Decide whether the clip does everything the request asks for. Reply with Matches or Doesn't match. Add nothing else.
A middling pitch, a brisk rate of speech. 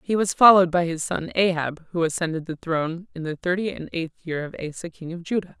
Matches